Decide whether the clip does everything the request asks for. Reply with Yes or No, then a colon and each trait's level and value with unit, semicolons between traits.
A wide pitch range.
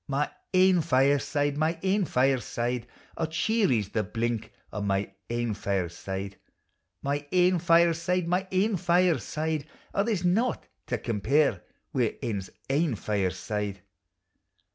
Yes: wide, 8.4 semitones